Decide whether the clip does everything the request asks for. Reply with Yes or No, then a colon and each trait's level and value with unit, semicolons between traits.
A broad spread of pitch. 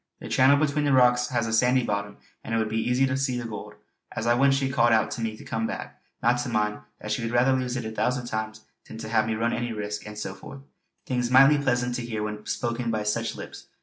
No: narrow, 2.5 semitones